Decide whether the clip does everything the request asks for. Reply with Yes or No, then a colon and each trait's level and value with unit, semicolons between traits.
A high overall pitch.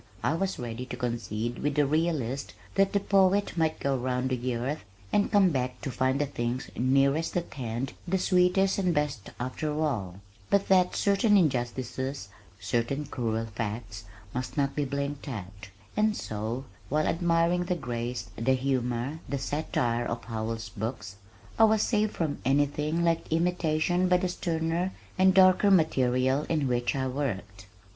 No: medium, 140 Hz